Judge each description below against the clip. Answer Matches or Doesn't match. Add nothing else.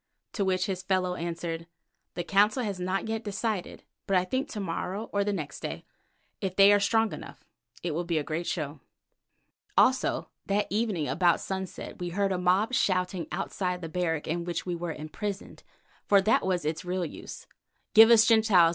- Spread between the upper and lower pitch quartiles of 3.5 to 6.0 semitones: Doesn't match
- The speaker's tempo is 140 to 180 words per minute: Doesn't match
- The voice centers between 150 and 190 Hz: Matches